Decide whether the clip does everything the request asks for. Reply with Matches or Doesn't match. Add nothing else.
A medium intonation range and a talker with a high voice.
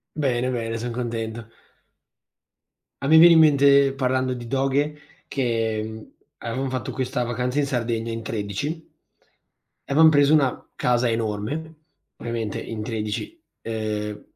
Doesn't match